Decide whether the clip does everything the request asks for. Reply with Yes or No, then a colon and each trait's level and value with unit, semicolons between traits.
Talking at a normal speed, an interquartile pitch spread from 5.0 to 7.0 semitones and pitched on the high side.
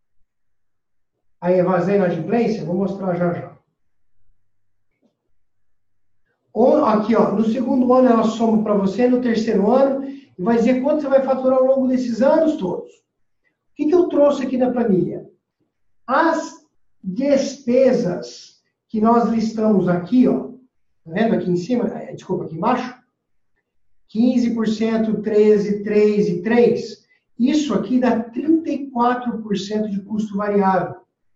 Yes: average, 130 wpm; wide, 5.4 semitones; high, 220 Hz